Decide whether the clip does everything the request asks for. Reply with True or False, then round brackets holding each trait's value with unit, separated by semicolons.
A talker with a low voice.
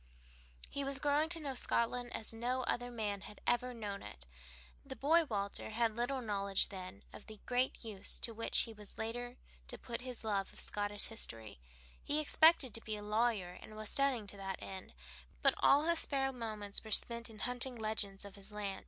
False (225 Hz)